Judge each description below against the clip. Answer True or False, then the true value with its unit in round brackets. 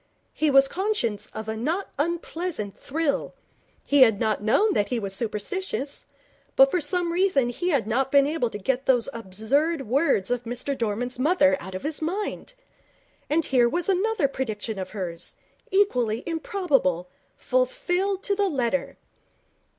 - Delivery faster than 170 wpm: False (155 wpm)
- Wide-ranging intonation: True (7.6 semitones)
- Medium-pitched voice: False (275 Hz)